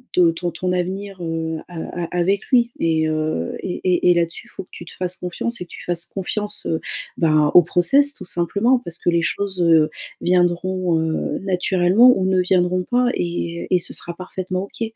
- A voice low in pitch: No, medium, 180 Hz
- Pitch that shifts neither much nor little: No, narrow, 2.0 semitones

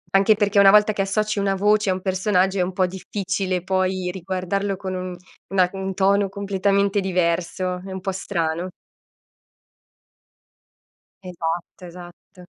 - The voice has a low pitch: No, high, 190 Hz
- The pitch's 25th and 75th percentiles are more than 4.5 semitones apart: No, narrow, 1.5 semitones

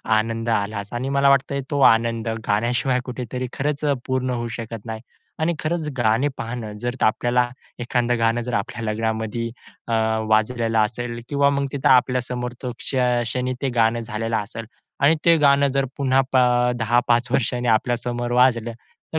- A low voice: Yes, low, 120 Hz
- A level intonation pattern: Yes, narrow, 2.3 semitones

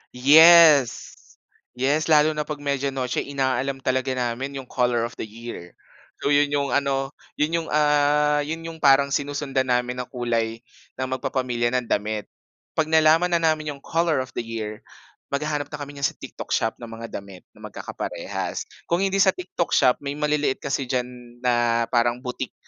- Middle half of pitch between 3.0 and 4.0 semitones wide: Yes, average, 3.3 semitones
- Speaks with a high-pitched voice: No, low, 135 Hz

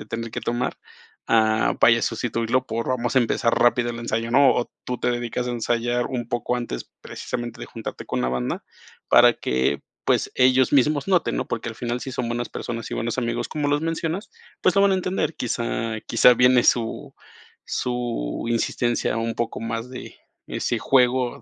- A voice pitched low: Yes, low, 120 Hz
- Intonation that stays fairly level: Yes, narrow, 1.7 semitones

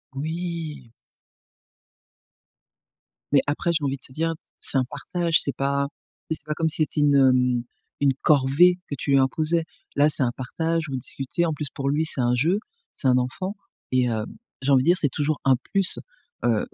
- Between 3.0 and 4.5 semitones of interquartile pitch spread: Yes, average, 3.5 semitones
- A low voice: No, medium, 145 Hz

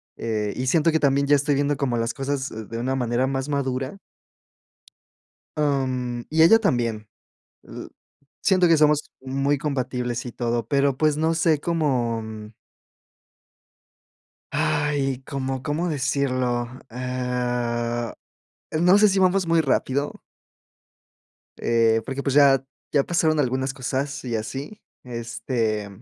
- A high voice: No, low, 135 Hz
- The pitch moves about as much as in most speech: Yes, average, 3.3 semitones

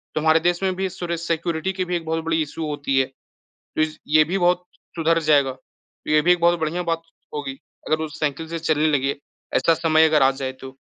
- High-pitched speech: No, medium, 160 Hz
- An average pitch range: No, narrow, 2.3 semitones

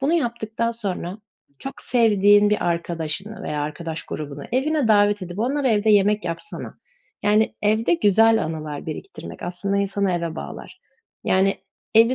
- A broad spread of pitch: No, average, 4.5 semitones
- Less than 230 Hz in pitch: Yes, high, 205 Hz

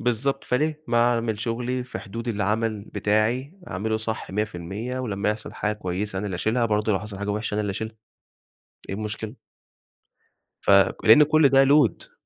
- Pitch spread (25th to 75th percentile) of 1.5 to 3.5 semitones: Yes, average, 2.9 semitones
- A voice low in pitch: Yes, low, 110 Hz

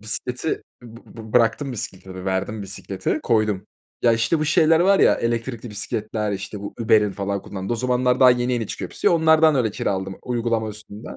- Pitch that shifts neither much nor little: Yes, average, 3.5 semitones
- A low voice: Yes, low, 115 Hz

